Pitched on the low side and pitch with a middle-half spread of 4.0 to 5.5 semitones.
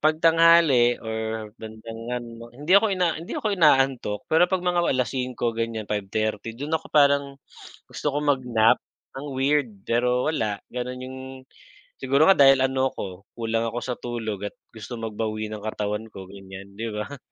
Yes: low, 120 Hz; average, 4.3 semitones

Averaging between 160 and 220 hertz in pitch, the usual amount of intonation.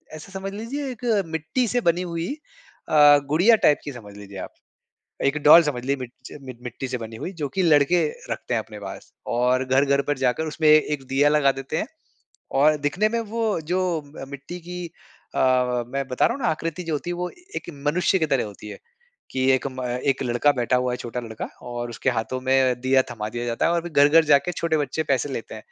No: medium, 145 Hz; average, 4.8 semitones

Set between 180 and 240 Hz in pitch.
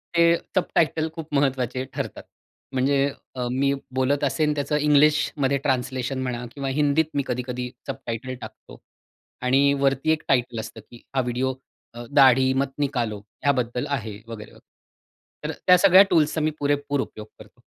No: low, 135 Hz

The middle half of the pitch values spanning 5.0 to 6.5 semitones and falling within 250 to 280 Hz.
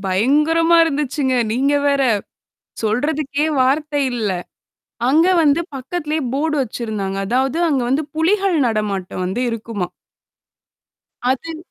Yes: average, 5.3 semitones; very high, 275 Hz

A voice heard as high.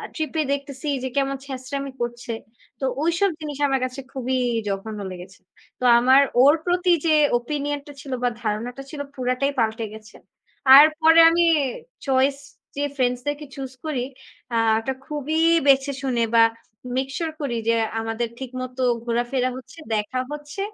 Yes: very high, 265 Hz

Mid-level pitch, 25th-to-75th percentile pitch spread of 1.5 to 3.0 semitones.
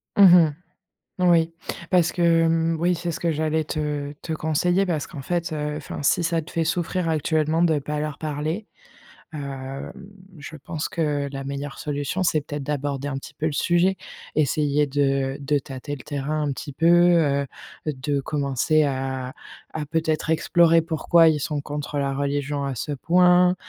Yes: medium, 150 Hz; average, 2.7 semitones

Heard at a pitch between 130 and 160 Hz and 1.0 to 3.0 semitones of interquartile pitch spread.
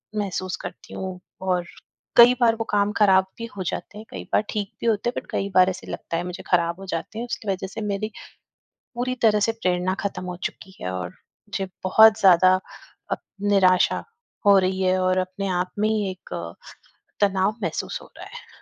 No: high, 190 Hz; narrow, 2.4 semitones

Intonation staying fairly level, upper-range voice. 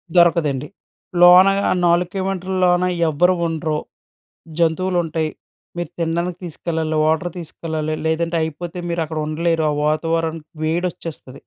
No: narrow, 1.9 semitones; medium, 165 Hz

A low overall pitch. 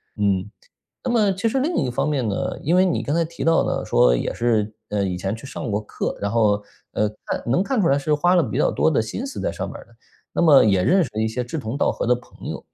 Yes: low, 125 Hz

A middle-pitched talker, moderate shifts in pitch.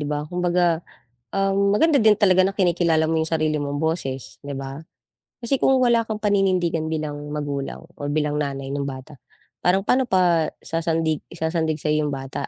Yes: medium, 160 Hz; average, 4.0 semitones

